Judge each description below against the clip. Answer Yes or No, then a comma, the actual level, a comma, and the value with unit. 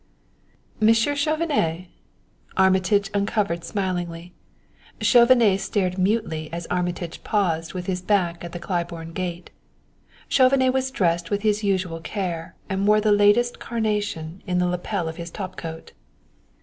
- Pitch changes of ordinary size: Yes, average, 3.6 semitones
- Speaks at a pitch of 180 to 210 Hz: Yes, high, 190 Hz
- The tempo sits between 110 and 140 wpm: Yes, slow, 135 wpm